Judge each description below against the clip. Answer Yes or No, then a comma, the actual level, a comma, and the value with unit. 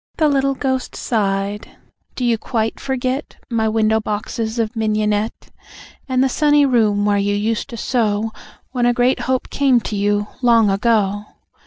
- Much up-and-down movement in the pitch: No, average, 3.4 semitones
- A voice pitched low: No, high, 225 Hz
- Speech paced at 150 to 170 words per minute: Yes, average, 160 wpm